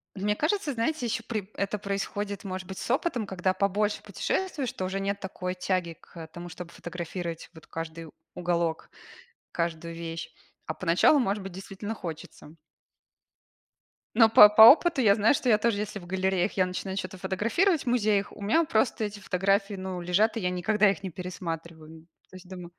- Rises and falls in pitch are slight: No, average, 3.2 semitones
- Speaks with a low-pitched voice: No, high, 190 Hz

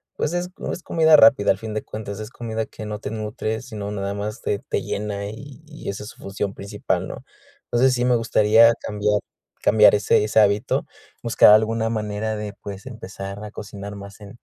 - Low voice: Yes, low, 105 Hz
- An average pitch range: No, narrow, 1.8 semitones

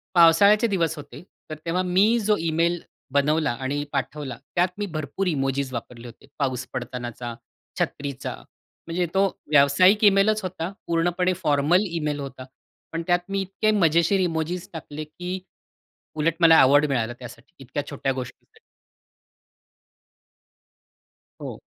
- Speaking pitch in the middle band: Yes, medium, 160 Hz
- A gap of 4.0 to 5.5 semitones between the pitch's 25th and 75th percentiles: Yes, average, 4.5 semitones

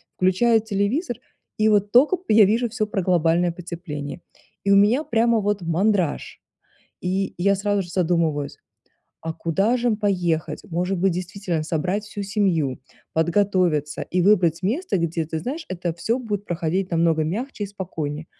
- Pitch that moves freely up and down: No, average, 3.7 semitones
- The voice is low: No, medium, 185 Hz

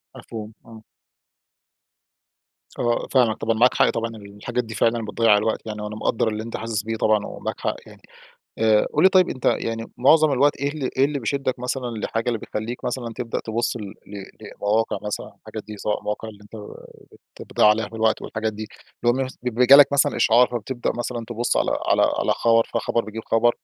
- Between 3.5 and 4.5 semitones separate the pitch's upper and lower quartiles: No, narrow, 2.4 semitones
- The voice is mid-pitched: No, low, 115 Hz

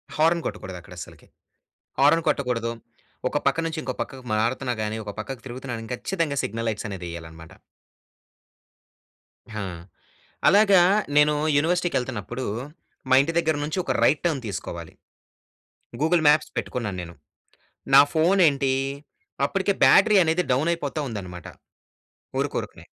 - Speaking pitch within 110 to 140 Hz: Yes, low, 135 Hz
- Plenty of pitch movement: Yes, wide, 6.6 semitones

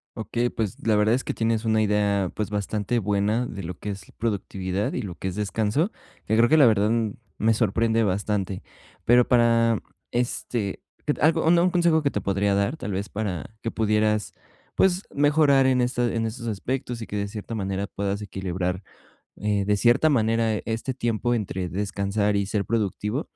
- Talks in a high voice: No, low, 110 Hz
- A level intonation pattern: No, average, 3.0 semitones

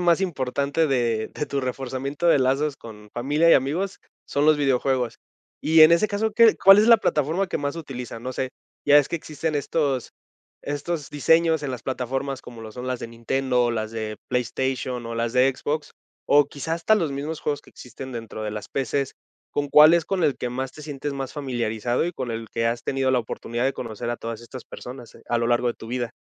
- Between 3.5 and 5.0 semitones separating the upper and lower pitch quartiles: Yes, average, 3.8 semitones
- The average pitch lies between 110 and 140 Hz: Yes, low, 135 Hz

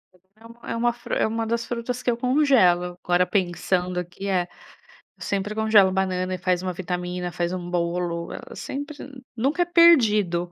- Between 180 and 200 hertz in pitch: Yes, high, 190 Hz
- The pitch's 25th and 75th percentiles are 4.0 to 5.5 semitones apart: Yes, average, 4.7 semitones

